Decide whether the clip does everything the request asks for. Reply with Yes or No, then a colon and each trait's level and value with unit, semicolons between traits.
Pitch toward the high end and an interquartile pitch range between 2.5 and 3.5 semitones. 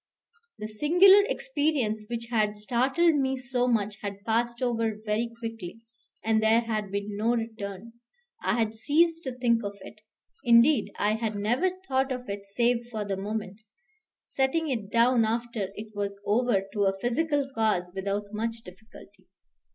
Yes: high, 225 Hz; average, 3.0 semitones